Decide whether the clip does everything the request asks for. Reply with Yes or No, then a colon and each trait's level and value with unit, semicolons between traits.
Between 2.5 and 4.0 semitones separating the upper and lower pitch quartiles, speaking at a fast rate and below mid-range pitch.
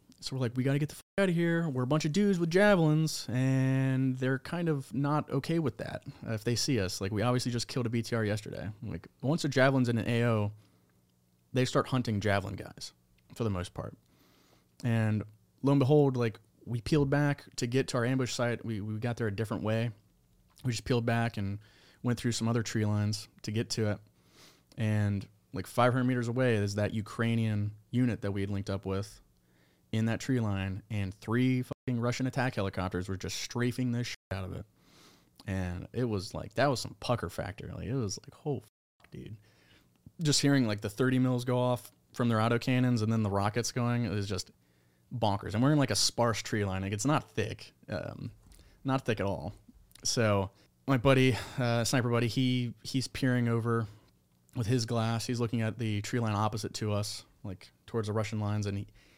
Yes: average, 3.7 semitones; fast, 210 wpm; low, 115 Hz